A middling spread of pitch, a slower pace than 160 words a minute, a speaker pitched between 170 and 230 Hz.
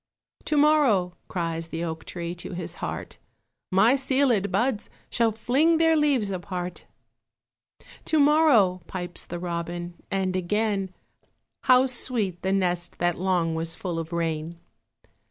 No: wide, 5.9 semitones; slow, 135 wpm; medium, 185 Hz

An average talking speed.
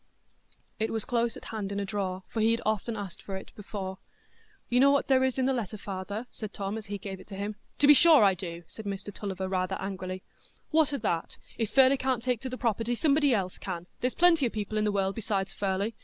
No: fast, 245 wpm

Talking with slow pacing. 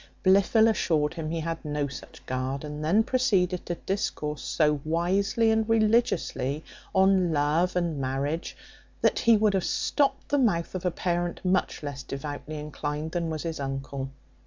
No: average, 160 wpm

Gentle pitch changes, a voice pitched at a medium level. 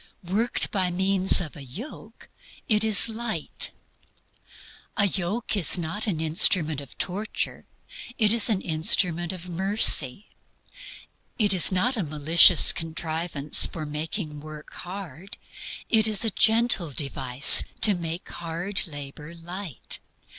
No: average, 4.5 semitones; medium, 175 Hz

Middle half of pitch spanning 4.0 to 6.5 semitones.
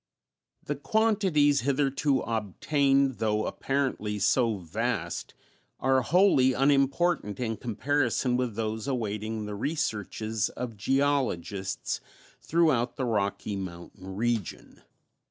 Yes: average, 4.7 semitones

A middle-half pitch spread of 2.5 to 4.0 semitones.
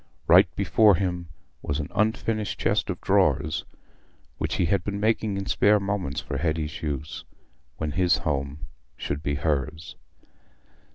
No: average, 5.2 semitones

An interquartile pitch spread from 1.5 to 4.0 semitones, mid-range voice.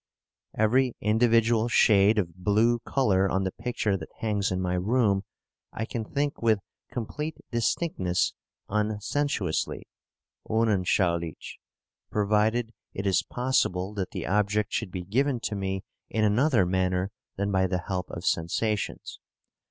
No: average, 3.5 semitones; low, 105 Hz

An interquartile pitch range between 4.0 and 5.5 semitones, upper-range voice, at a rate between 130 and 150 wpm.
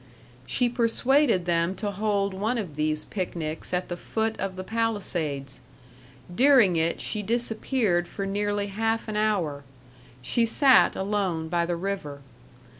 Yes: average, 4.5 semitones; high, 200 Hz; average, 140 wpm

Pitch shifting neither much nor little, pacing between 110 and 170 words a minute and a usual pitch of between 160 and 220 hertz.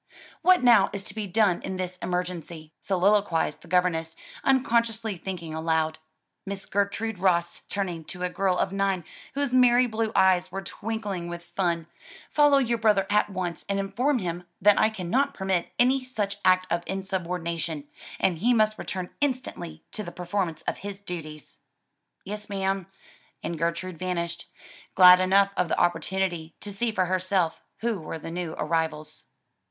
Yes: average, 3.4 semitones; average, 160 wpm; high, 190 Hz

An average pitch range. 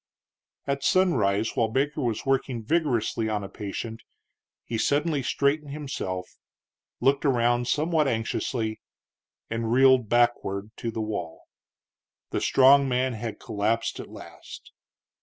Yes: average, 3.9 semitones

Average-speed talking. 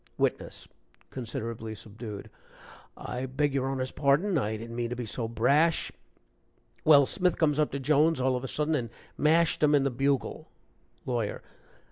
Yes: average, 165 wpm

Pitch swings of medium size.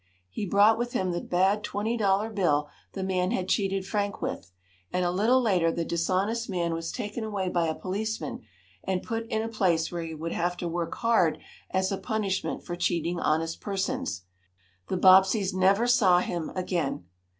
Yes: average, 3.3 semitones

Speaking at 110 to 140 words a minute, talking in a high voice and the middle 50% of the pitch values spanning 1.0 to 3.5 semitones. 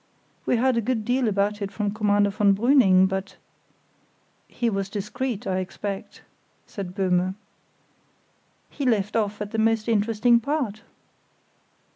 Yes: slow, 135 wpm; high, 210 Hz; average, 2.8 semitones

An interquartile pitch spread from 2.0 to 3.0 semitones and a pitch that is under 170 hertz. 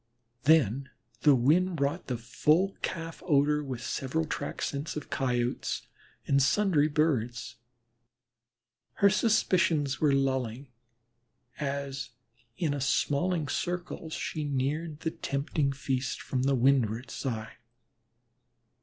No: average, 3.4 semitones; medium, 140 Hz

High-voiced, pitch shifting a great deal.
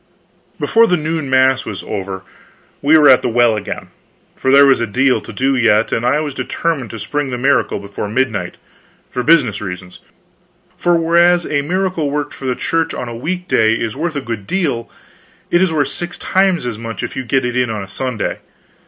No: low, 130 Hz; wide, 5.7 semitones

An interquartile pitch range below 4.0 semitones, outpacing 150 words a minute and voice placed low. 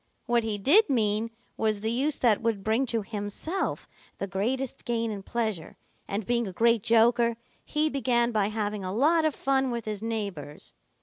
No: average, 2.8 semitones; average, 180 wpm; high, 230 Hz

